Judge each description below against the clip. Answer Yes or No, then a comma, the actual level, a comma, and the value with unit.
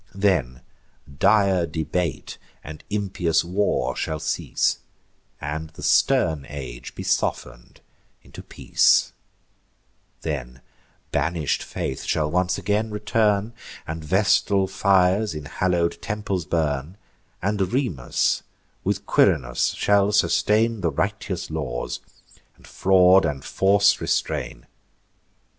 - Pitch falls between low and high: No, very low, 90 Hz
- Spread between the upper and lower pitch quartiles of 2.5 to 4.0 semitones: No, average, 4.7 semitones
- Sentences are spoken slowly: Yes, slow, 105 wpm